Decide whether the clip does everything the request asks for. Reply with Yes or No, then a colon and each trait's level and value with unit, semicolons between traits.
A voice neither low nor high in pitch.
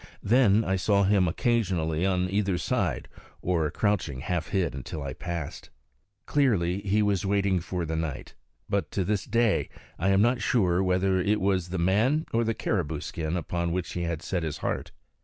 No: very low, 95 Hz